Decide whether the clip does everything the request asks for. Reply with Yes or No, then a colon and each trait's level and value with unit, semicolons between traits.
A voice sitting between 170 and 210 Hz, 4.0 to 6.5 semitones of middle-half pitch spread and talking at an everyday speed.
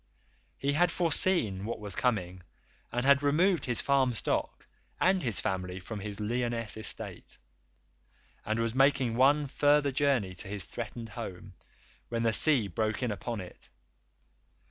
No: low, 115 Hz; average, 5.0 semitones; average, 145 wpm